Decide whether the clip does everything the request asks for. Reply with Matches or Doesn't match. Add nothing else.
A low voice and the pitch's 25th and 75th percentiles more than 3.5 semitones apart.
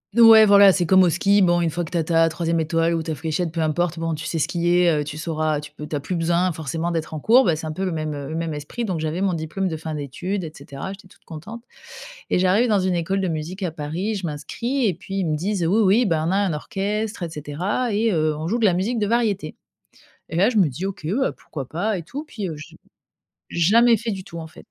Doesn't match